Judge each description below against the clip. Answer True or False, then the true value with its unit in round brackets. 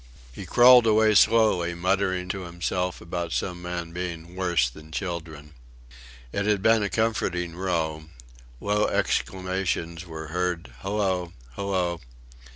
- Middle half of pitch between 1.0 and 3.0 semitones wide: True (2.7 semitones)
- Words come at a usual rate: False (125 wpm)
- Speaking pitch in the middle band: False (90 Hz)